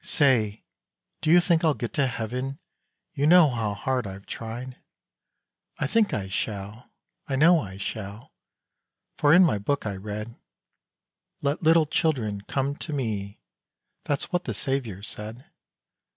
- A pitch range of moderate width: No, wide, 5.7 semitones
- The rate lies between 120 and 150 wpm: Yes, average, 145 wpm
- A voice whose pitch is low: Yes, low, 125 Hz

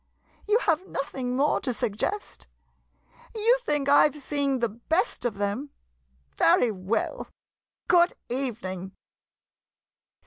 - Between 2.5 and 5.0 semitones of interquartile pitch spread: No, wide, 5.6 semitones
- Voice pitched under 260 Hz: No, very high, 270 Hz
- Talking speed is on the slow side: Yes, slow, 115 wpm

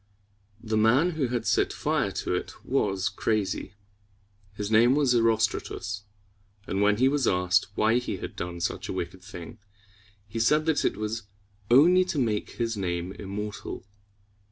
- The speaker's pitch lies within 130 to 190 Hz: No, low, 110 Hz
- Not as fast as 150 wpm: No, average, 165 wpm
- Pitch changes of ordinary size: Yes, average, 3.9 semitones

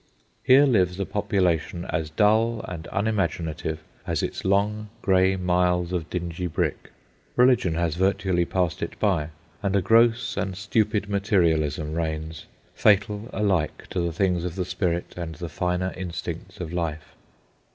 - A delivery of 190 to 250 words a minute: No, average, 145 wpm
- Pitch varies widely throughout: No, average, 3.1 semitones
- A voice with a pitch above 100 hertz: No, very low, 90 Hz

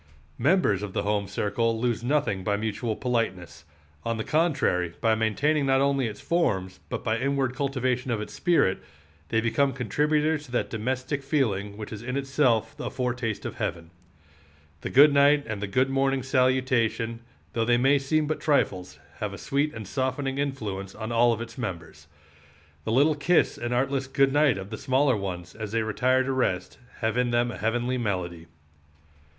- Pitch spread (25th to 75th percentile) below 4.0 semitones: No, average, 4.3 semitones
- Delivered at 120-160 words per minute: No, average, 180 wpm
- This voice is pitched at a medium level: No, low, 120 Hz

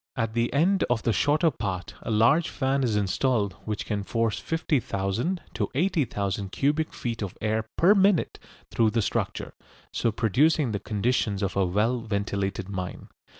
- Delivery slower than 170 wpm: Yes, average, 160 wpm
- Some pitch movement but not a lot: No, wide, 5.7 semitones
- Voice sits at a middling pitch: No, low, 115 Hz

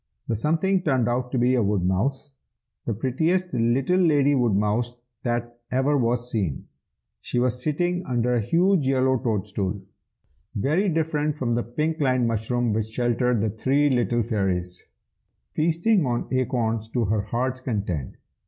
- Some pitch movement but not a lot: Yes, average, 4.4 semitones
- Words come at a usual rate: Yes, average, 145 wpm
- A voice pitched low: Yes, low, 125 Hz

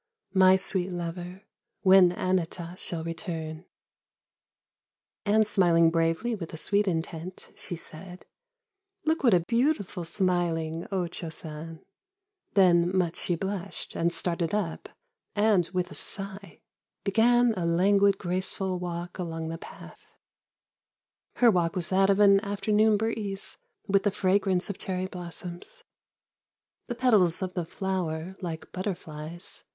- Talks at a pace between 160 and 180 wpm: No, slow, 135 wpm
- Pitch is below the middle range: No, medium, 185 Hz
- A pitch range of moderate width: Yes, average, 3.0 semitones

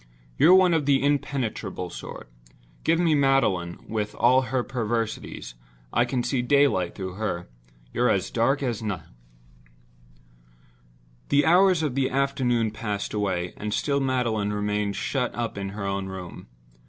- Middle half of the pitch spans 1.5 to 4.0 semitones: No, average, 5.1 semitones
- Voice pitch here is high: No, low, 120 Hz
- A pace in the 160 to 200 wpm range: No, average, 145 wpm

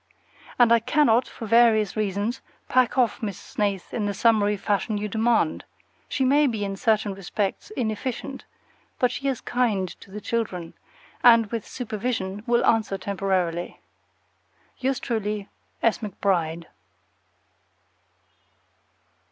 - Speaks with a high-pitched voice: Yes, high, 215 Hz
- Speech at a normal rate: No, slow, 125 wpm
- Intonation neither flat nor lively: Yes, average, 3.2 semitones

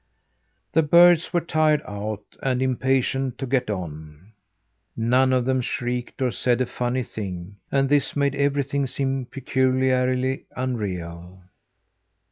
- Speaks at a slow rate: Yes, slow, 125 wpm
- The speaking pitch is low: Yes, low, 130 Hz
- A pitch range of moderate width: Yes, average, 3.4 semitones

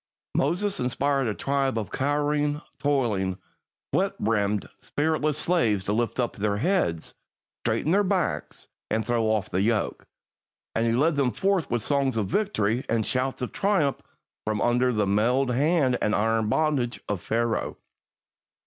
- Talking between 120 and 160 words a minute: Yes, average, 150 wpm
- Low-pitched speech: Yes, low, 125 Hz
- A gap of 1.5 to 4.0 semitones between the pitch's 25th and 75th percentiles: No, average, 5.1 semitones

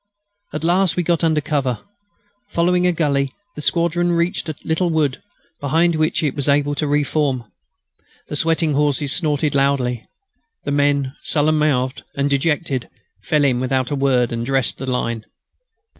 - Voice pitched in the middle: Yes, medium, 145 Hz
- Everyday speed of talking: Yes, average, 160 wpm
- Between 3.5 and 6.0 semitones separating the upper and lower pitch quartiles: No, average, 2.9 semitones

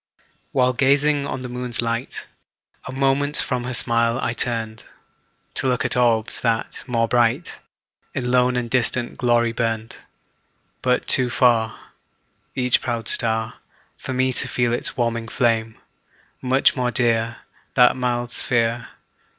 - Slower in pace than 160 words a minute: Yes, average, 140 wpm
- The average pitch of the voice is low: Yes, low, 120 Hz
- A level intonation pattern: Yes, narrow, 1.6 semitones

